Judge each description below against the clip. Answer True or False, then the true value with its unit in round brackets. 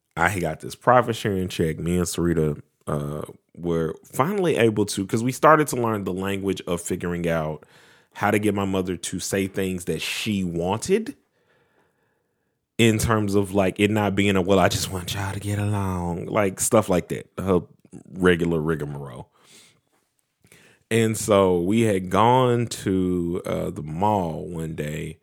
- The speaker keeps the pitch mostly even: False (3.5 semitones)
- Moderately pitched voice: False (95 Hz)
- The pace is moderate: True (165 wpm)